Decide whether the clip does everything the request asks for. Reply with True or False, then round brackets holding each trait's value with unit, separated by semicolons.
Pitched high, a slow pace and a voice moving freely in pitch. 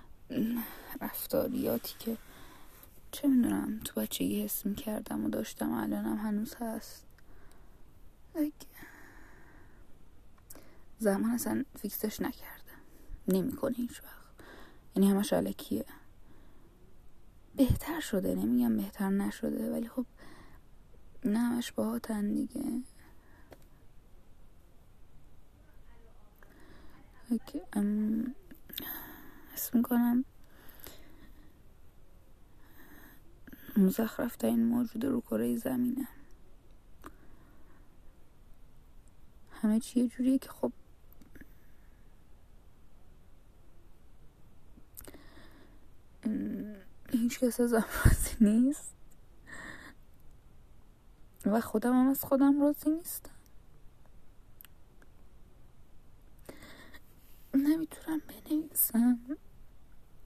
False (240 Hz; 65 wpm; 3.7 semitones)